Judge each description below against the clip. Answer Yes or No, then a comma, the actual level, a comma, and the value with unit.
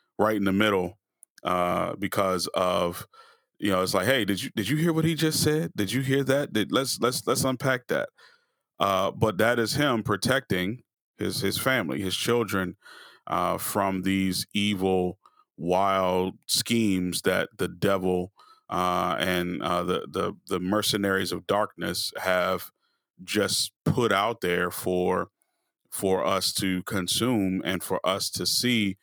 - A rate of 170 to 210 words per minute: No, average, 155 wpm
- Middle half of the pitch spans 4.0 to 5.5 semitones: Yes, average, 4.5 semitones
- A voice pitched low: Yes, low, 100 Hz